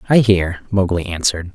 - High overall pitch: No, very low, 95 Hz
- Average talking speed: Yes, average, 155 wpm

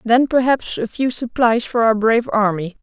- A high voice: Yes, high, 230 Hz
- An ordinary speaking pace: Yes, average, 190 wpm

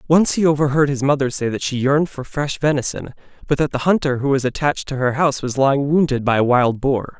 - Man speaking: Yes, male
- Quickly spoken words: Yes, fast, 240 wpm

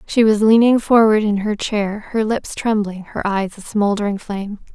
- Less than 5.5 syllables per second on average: Yes, 4.7 syllables/s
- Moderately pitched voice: No, high, 210 Hz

